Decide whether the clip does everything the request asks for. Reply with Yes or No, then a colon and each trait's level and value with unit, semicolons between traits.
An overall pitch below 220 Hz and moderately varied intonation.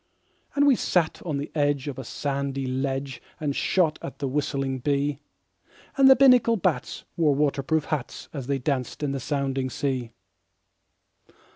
No: medium, 140 Hz; narrow, 2.3 semitones